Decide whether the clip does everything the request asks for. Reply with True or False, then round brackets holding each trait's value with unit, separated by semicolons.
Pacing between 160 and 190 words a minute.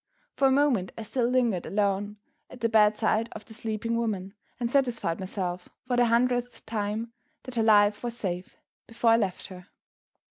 True (175 wpm)